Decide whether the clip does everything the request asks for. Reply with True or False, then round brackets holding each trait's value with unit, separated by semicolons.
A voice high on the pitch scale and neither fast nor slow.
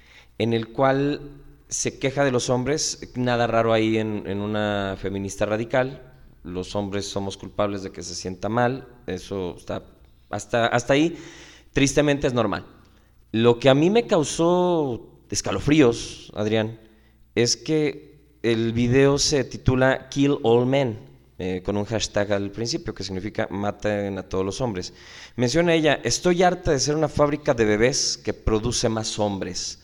False (115 Hz; 155 wpm)